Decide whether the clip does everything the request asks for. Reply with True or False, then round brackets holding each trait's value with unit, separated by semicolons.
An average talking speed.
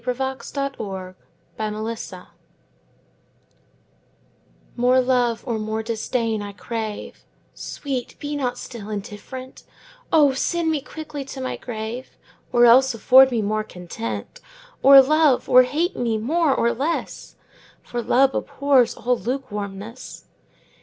False (120 wpm)